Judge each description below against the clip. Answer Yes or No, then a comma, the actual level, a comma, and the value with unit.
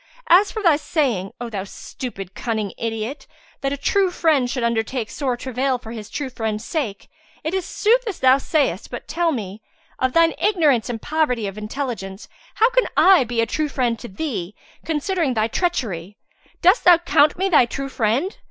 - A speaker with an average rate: Yes, average, 185 wpm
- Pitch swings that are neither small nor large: No, wide, 6.3 semitones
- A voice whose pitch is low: No, very high, 260 Hz